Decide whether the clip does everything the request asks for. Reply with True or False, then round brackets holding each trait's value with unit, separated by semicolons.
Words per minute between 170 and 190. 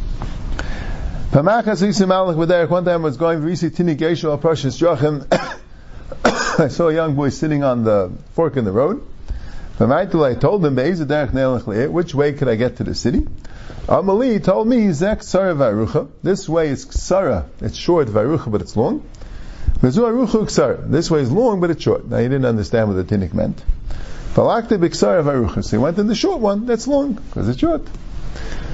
False (140 wpm)